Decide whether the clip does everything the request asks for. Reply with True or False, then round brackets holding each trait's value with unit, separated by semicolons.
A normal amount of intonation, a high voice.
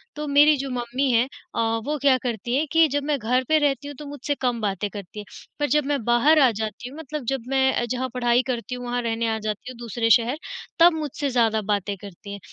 True (3.9 semitones; 250 Hz)